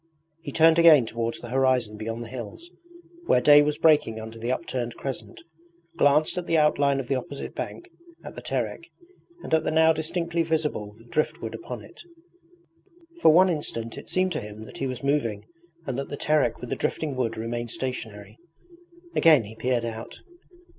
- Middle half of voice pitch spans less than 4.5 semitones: No, average, 5.3 semitones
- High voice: No, low, 135 Hz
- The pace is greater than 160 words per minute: Yes, average, 180 wpm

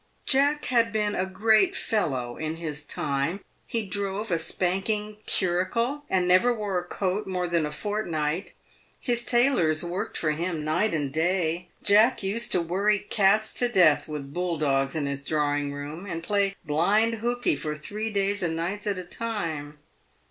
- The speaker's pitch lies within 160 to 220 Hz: Yes, medium, 185 Hz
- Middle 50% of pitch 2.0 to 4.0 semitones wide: No, average, 5.2 semitones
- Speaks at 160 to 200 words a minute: Yes, average, 170 wpm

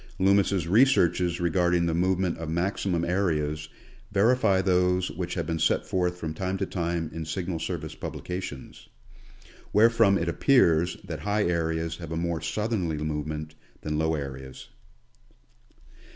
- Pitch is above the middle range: No, very low, 85 Hz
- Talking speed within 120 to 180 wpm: Yes, average, 150 wpm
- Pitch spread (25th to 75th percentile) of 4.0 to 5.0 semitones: No, average, 2.7 semitones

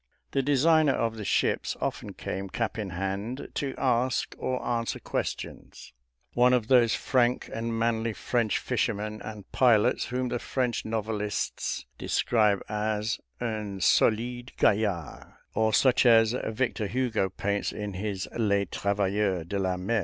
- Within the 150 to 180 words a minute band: No, average, 140 wpm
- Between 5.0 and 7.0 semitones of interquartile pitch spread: No, average, 3.1 semitones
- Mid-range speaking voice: No, low, 110 Hz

